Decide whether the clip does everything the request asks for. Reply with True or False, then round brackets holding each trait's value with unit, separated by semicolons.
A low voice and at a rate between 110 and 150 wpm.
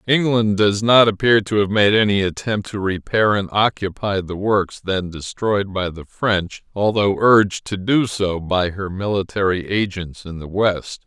False (100 Hz; 175 wpm)